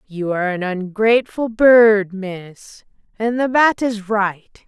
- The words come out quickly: No, average, 140 wpm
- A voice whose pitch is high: Yes, high, 210 Hz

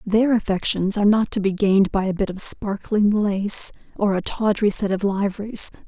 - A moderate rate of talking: Yes, average, 195 wpm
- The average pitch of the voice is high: Yes, high, 200 Hz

